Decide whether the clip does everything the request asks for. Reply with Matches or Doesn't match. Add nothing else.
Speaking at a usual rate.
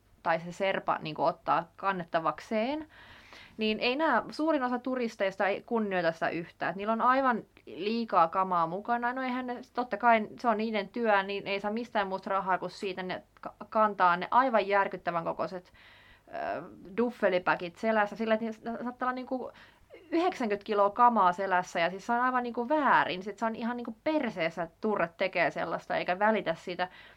Doesn't match